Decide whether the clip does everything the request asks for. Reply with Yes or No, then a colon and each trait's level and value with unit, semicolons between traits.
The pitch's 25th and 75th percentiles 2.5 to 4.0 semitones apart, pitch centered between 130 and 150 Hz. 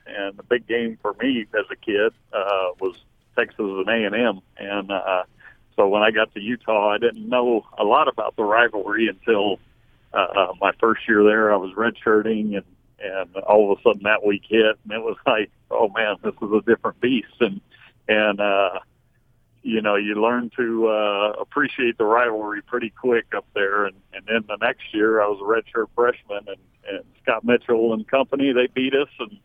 No: average, 2.8 semitones; low, 110 Hz